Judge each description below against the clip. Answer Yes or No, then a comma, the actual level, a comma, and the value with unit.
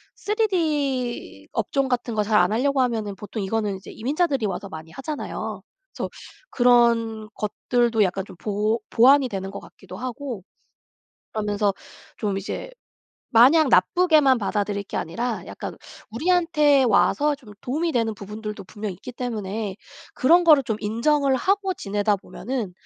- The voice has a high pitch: Yes, high, 235 Hz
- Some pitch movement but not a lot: Yes, average, 5.0 semitones